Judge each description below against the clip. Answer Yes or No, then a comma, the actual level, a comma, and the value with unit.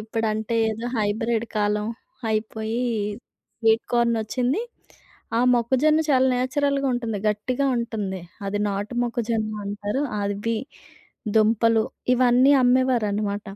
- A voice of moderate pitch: No, high, 225 Hz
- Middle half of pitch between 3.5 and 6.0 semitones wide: No, average, 2.7 semitones